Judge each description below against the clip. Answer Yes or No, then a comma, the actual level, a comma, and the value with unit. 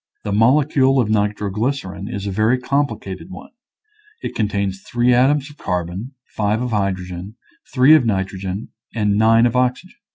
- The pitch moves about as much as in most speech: Yes, average, 4.3 semitones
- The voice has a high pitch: No, low, 110 Hz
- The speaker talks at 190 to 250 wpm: No, average, 150 wpm